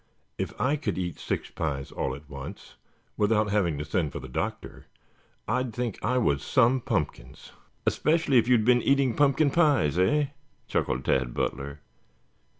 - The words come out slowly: No, average, 160 wpm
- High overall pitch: No, low, 105 Hz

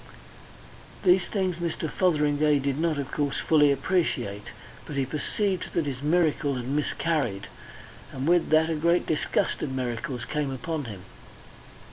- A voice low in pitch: No, medium, 150 Hz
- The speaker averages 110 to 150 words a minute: Yes, average, 145 wpm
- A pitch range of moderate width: Yes, average, 3.8 semitones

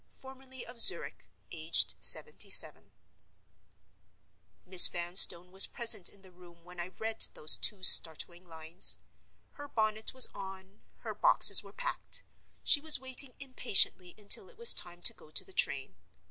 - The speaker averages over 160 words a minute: No, average, 145 wpm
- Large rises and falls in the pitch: Yes, wide, 6.7 semitones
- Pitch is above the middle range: Yes, high, 195 Hz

